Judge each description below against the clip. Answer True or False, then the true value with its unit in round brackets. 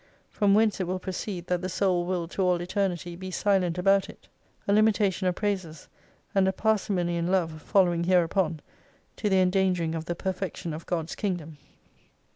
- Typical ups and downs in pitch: False (2.1 semitones)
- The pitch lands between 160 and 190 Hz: True (185 Hz)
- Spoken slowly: False (180 wpm)